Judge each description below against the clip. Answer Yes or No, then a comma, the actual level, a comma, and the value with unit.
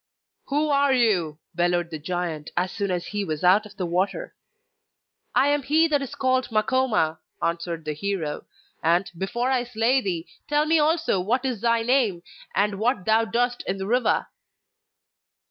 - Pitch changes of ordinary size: No, wide, 6.5 semitones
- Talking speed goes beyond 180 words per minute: No, average, 170 wpm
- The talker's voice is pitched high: Yes, high, 210 Hz